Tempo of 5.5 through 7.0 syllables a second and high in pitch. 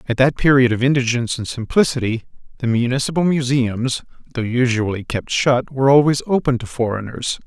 No: 5.8 syllables/s; low, 125 Hz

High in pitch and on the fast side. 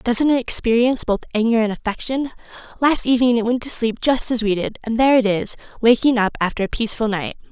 Yes: high, 235 Hz; fast, 215 wpm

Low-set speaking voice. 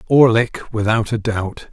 Yes: low, 110 Hz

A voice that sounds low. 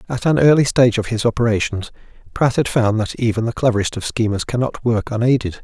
Yes: low, 115 Hz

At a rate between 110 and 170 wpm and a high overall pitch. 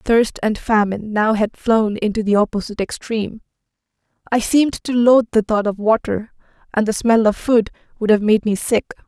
No: average, 185 wpm; high, 215 Hz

